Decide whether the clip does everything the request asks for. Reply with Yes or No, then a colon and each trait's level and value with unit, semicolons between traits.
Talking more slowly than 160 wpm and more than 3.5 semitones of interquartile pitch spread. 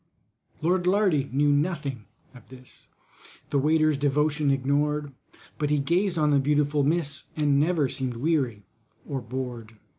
No: average, 140 wpm; narrow, 2.4 semitones